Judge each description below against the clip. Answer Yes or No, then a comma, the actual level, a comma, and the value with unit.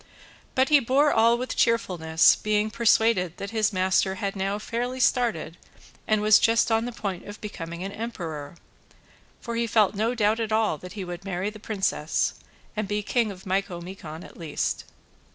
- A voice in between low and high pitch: No, high, 210 Hz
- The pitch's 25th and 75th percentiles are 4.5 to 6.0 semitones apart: No, average, 3.8 semitones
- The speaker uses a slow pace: No, average, 175 wpm